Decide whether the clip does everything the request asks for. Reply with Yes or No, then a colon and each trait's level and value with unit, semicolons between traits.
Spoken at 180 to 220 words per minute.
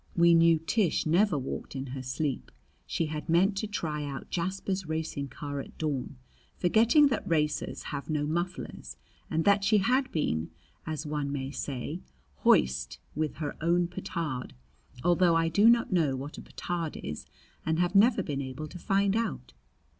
No: average, 165 wpm